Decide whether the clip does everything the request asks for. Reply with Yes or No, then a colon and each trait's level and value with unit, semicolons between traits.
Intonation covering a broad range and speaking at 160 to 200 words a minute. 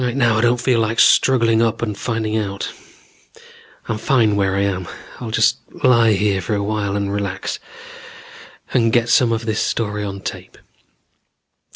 No: narrow, 2.4 semitones; average, 170 wpm